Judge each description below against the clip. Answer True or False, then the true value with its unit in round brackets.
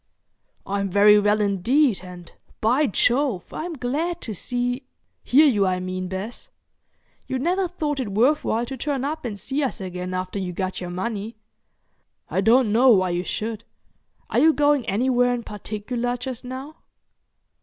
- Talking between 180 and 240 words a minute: False (160 wpm)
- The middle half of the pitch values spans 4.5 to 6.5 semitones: True (5.2 semitones)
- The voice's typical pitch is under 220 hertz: False (235 Hz)